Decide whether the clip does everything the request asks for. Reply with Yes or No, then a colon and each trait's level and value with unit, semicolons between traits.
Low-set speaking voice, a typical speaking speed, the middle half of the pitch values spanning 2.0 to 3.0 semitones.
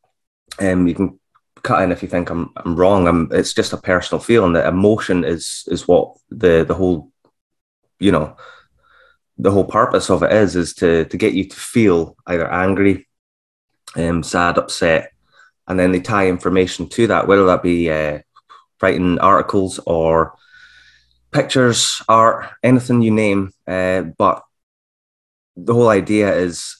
Yes: very low, 90 Hz; average, 160 wpm; narrow, 2.6 semitones